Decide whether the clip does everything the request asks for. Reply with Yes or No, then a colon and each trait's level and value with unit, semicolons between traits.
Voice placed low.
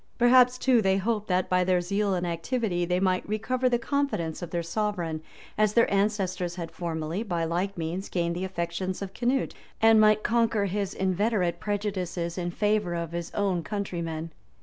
No: high, 190 Hz